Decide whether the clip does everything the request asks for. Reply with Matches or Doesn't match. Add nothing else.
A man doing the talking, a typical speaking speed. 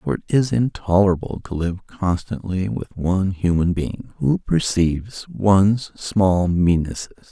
Doesn't match